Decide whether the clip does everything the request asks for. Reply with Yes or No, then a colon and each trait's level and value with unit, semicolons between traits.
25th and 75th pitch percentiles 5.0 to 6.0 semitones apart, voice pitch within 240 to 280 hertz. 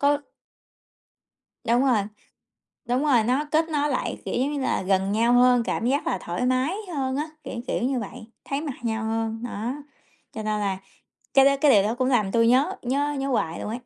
No: average, 3.8 semitones; high, 245 Hz